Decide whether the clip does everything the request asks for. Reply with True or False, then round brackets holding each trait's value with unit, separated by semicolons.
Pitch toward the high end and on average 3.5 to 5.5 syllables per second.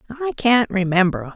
True (210 Hz; 4.6 syllables/s)